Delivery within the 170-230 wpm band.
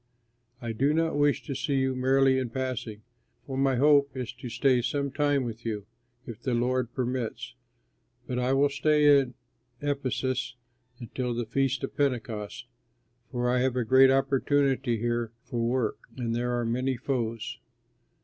No: average, 160 wpm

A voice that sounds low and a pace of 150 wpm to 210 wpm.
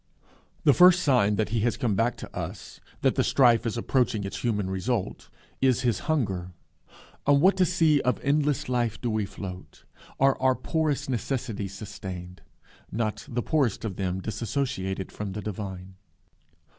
Yes: low, 115 Hz; average, 160 wpm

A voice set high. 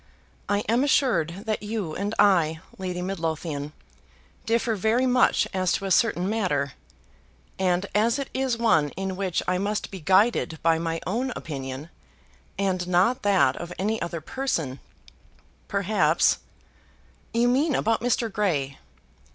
Yes: high, 195 Hz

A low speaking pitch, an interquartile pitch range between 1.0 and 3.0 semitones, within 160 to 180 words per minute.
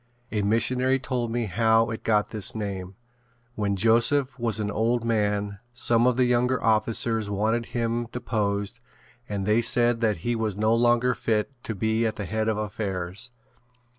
Yes: low, 110 Hz; narrow, 2.4 semitones; average, 165 wpm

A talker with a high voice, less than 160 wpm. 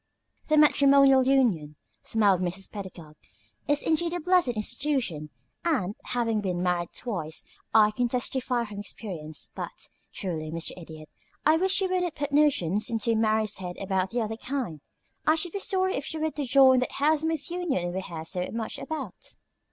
No: high, 230 Hz; average, 165 wpm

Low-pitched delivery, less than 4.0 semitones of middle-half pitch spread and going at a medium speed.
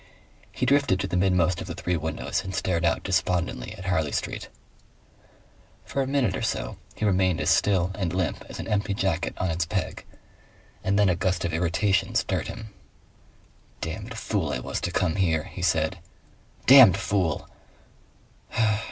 Yes: very low, 90 Hz; average, 3.0 semitones; average, 170 wpm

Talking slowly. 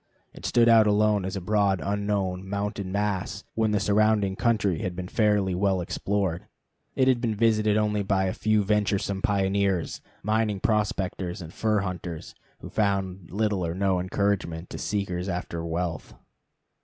No: average, 155 wpm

